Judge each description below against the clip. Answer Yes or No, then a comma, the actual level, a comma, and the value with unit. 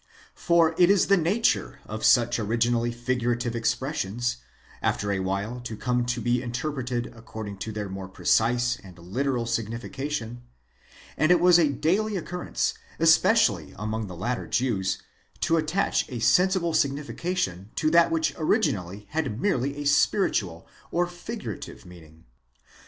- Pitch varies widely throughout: Yes, wide, 6.4 semitones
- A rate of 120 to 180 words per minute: Yes, average, 140 wpm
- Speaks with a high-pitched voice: No, low, 120 Hz